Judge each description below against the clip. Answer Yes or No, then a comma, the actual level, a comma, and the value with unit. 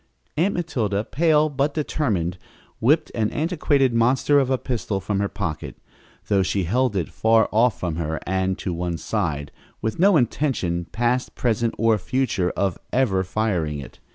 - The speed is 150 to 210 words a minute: Yes, average, 160 wpm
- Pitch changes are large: Yes, wide, 6.2 semitones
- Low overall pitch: Yes, low, 110 Hz